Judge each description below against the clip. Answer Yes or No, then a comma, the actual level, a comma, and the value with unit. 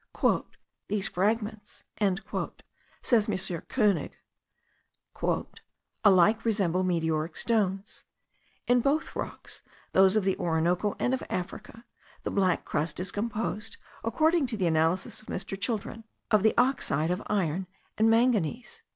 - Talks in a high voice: Yes, high, 205 Hz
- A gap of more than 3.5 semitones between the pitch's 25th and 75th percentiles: Yes, average, 3.9 semitones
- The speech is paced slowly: Yes, slow, 120 wpm